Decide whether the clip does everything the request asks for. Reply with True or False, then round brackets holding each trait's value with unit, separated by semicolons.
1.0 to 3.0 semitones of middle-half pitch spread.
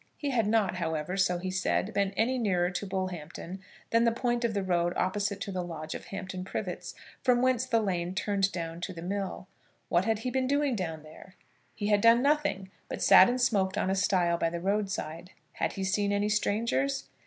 False (3.9 semitones)